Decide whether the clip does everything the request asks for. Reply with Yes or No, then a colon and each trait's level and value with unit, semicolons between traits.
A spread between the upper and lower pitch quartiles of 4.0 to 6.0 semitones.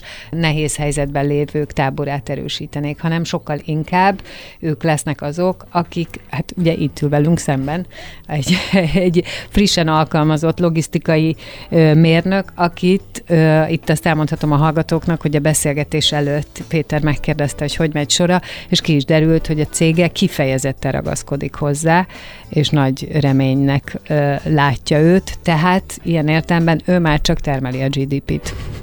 No: narrow, 2.5 semitones